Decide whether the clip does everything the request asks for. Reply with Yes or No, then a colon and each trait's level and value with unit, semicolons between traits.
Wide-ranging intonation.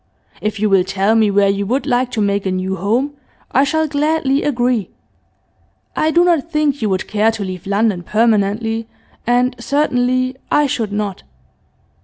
No: average, 5.0 semitones